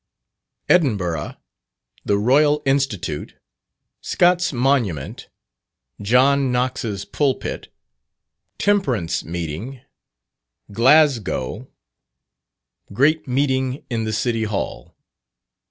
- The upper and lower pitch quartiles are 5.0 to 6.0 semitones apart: Yes, wide, 5.5 semitones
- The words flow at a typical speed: No, slow, 70 wpm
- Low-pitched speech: Yes, low, 125 Hz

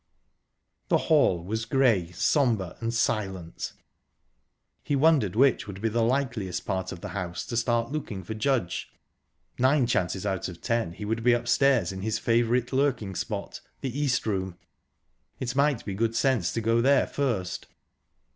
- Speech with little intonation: No, average, 5.1 semitones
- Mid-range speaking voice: No, low, 115 Hz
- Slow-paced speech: No, average, 155 wpm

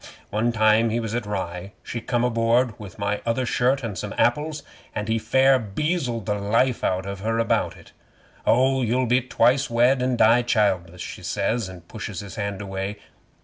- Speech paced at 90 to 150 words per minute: No, average, 190 wpm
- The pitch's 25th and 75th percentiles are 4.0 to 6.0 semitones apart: No, average, 3.4 semitones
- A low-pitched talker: Yes, low, 115 Hz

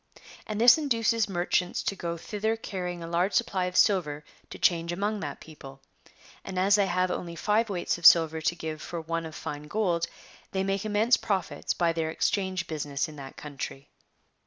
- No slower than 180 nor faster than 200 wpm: Yes, average, 185 wpm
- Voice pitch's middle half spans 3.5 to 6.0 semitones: Yes, average, 3.9 semitones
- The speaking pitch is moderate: Yes, medium, 175 Hz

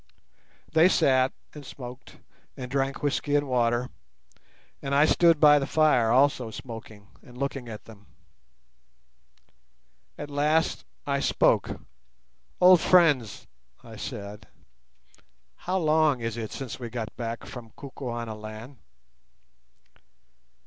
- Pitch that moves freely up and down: No, average, 4.0 semitones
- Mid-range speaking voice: No, low, 130 Hz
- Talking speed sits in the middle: No, slow, 115 wpm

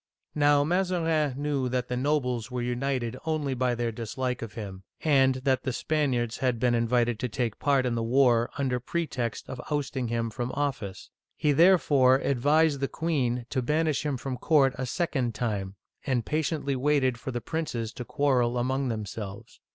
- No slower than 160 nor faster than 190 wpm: Yes, average, 175 wpm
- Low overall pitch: Yes, low, 130 Hz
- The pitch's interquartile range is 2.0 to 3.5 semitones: Yes, average, 3.2 semitones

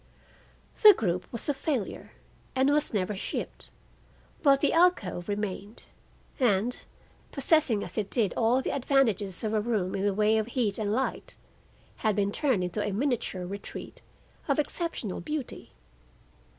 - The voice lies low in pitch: No, high, 220 Hz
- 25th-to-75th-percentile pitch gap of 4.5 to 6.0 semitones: Yes, average, 5.2 semitones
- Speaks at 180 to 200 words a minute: No, average, 150 wpm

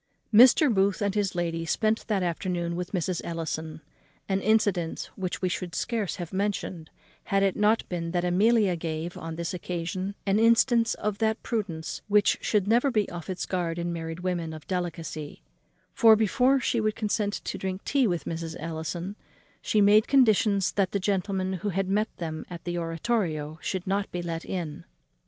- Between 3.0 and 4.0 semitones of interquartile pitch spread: Yes, average, 3.7 semitones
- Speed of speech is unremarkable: Yes, average, 180 wpm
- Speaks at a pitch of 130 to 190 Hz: Yes, medium, 185 Hz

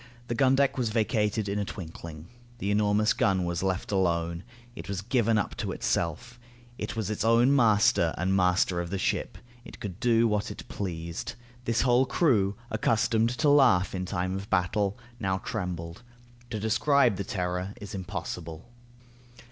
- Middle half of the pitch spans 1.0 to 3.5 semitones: No, average, 3.9 semitones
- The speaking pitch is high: No, low, 100 Hz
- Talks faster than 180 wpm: No, average, 165 wpm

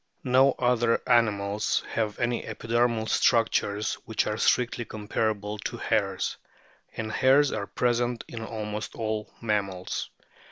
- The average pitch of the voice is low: Yes, low, 110 Hz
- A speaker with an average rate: No, slow, 120 wpm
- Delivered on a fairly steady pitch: Yes, narrow, 2.2 semitones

